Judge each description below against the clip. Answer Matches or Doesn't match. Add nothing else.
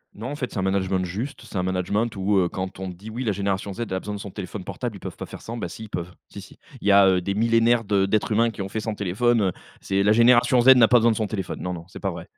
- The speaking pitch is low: Matches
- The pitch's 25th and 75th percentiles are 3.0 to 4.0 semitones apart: Matches